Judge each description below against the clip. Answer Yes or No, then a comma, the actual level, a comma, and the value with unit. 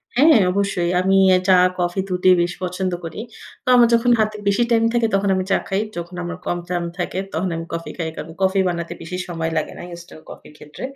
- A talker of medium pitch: Yes, medium, 180 Hz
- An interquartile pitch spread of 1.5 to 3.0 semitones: Yes, narrow, 2.6 semitones